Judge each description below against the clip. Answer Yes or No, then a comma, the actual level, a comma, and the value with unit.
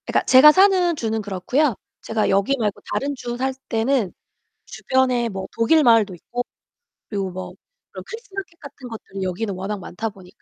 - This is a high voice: Yes, high, 230 Hz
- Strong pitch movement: Yes, wide, 5.8 semitones